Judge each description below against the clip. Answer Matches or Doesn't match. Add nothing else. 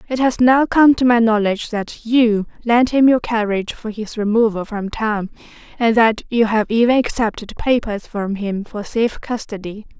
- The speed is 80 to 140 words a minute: Doesn't match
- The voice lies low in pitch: Doesn't match